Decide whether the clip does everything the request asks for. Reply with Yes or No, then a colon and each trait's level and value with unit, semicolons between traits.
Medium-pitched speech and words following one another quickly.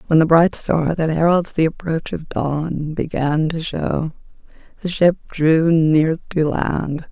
No: medium, 160 Hz; average, 160 wpm